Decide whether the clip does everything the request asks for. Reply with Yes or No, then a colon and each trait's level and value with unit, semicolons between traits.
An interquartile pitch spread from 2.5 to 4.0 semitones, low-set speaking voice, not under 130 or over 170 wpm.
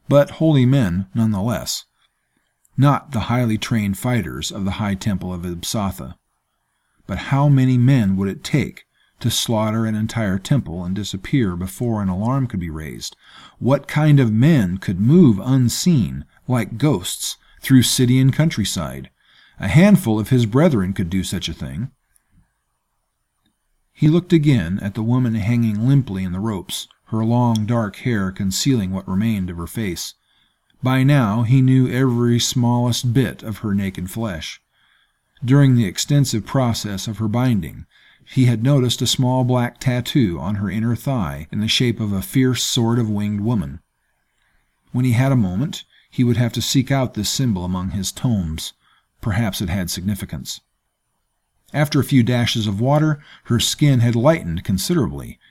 No: average, 4.5 semitones; low, 115 Hz; average, 165 wpm